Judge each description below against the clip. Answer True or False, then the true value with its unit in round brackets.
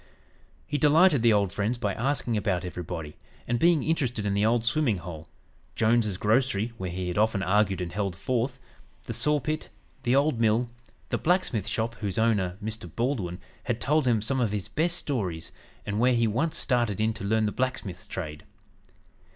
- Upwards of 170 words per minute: True (185 wpm)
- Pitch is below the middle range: True (110 Hz)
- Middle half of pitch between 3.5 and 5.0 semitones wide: True (4.4 semitones)